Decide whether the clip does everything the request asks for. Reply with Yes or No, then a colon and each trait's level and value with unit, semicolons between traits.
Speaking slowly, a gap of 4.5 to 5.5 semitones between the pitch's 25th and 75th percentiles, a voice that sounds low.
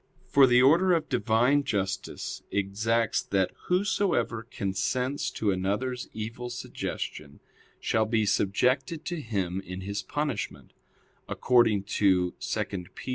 Yes: slow, 120 wpm; average, 4.8 semitones; low, 115 Hz